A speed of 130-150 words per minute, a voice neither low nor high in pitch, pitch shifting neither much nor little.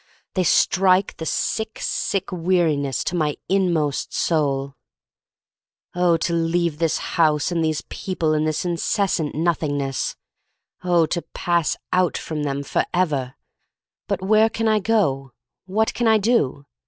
Yes: average, 140 wpm; medium, 170 Hz; average, 3.8 semitones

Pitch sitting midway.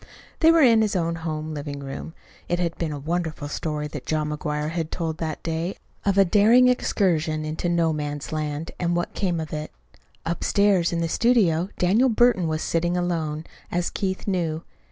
Yes: medium, 165 Hz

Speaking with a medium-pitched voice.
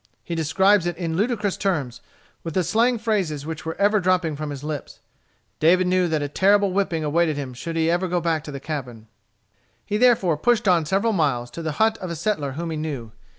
Yes: medium, 170 Hz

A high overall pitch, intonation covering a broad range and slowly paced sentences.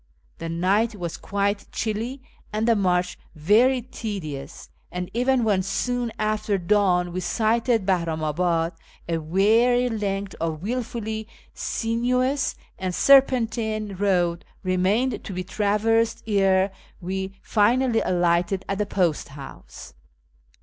No: high, 200 Hz; average, 4.1 semitones; slow, 115 wpm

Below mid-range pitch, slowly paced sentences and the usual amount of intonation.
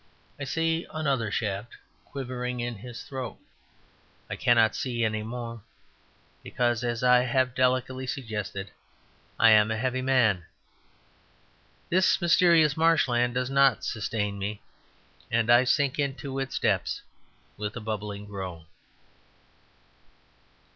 Yes: low, 120 Hz; slow, 120 wpm; average, 3.3 semitones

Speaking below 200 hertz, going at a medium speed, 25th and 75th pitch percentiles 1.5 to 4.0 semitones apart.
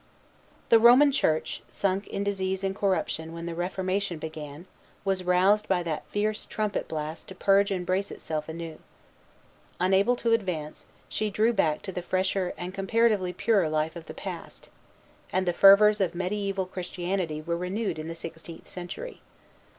Yes: medium, 185 Hz; average, 160 wpm; average, 3.1 semitones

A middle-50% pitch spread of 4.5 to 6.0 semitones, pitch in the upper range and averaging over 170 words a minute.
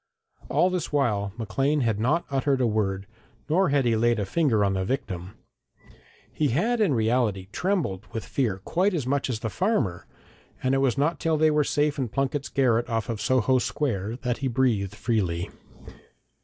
No: wide, 5.4 semitones; low, 125 Hz; average, 180 wpm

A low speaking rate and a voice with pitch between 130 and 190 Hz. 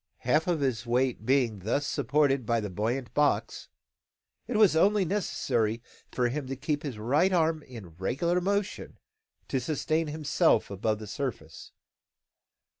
No: average, 145 wpm; low, 135 Hz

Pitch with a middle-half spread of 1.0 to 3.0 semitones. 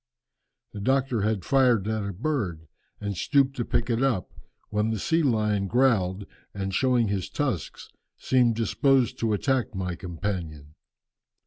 No: average, 4.9 semitones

